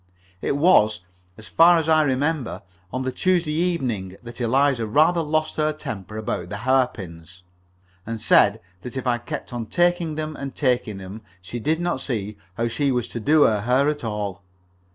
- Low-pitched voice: Yes, low, 125 Hz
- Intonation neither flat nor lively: No, wide, 6.0 semitones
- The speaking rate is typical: Yes, average, 180 wpm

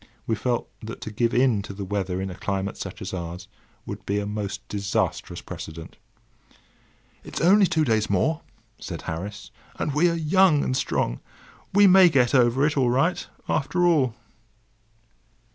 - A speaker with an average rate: Yes, average, 165 wpm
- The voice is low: Yes, low, 115 Hz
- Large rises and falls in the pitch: Yes, wide, 7.5 semitones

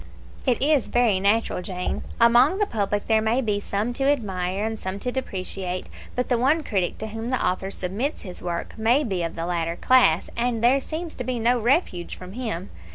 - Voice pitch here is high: Yes, high, 220 Hz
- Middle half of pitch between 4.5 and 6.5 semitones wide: Yes, average, 5.0 semitones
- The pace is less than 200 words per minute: No, fast, 205 wpm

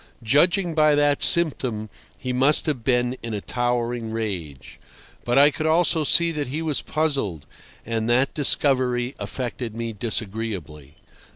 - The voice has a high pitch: No, low, 125 Hz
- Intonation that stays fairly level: No, average, 4.7 semitones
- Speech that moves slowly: No, average, 145 wpm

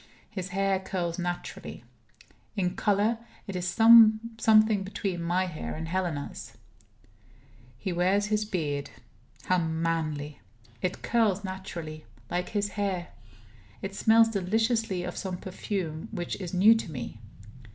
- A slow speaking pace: Yes, slow, 125 wpm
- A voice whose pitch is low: No, medium, 185 Hz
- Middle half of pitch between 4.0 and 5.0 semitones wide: No, average, 3.3 semitones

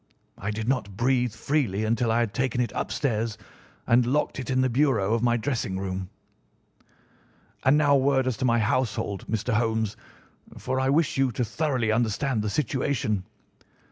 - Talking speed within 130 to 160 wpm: No, average, 170 wpm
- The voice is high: No, low, 120 Hz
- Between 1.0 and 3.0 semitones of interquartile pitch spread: No, average, 3.4 semitones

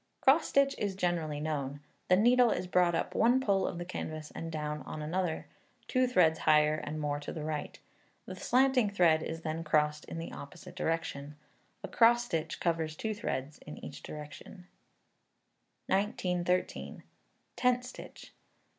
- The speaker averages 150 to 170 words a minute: Yes, average, 160 wpm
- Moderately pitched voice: Yes, medium, 165 Hz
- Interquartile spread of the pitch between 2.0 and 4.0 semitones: No, average, 5.2 semitones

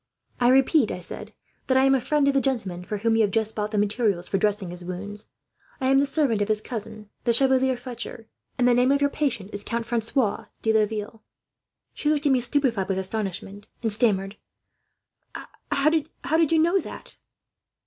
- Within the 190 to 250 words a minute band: Yes, average, 200 wpm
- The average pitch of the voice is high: Yes, high, 230 Hz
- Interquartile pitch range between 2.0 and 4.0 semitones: No, average, 4.4 semitones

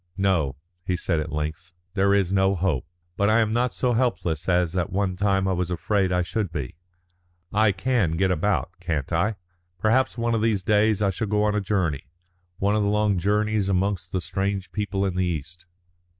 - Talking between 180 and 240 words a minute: Yes, fast, 205 wpm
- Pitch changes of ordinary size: Yes, average, 3.0 semitones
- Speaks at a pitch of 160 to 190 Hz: No, very low, 95 Hz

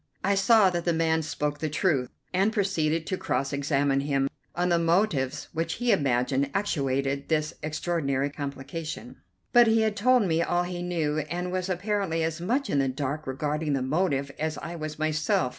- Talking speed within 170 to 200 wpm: Yes, average, 180 wpm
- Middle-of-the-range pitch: Yes, medium, 160 Hz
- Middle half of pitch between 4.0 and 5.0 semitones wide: Yes, average, 4.3 semitones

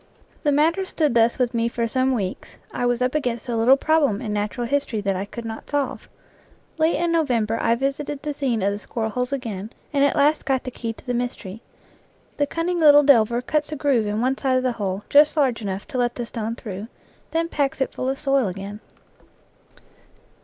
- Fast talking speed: Yes, fast, 215 wpm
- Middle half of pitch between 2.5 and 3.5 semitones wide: No, average, 4.1 semitones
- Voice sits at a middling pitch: No, very high, 250 Hz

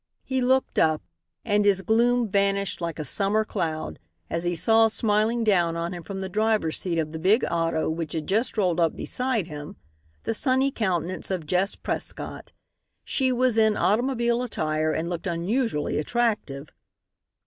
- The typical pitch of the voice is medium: No, high, 195 Hz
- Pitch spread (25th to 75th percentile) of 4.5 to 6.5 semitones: Yes, average, 5.2 semitones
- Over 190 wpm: No, average, 165 wpm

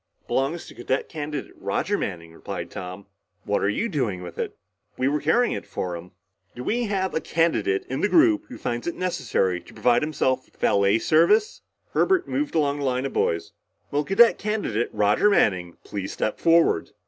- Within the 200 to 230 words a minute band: No, average, 185 wpm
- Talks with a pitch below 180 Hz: Yes, low, 135 Hz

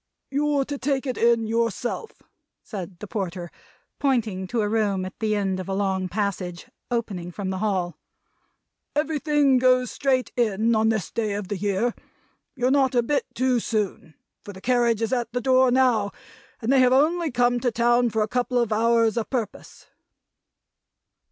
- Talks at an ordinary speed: Yes, average, 170 wpm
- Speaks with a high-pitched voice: Yes, high, 230 Hz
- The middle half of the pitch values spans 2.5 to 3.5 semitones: No, average, 3.9 semitones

